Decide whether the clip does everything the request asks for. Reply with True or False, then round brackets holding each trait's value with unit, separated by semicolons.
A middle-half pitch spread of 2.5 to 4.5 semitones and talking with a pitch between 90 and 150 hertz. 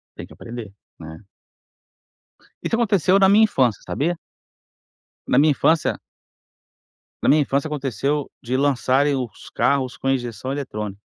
True (3.8 semitones; 135 Hz)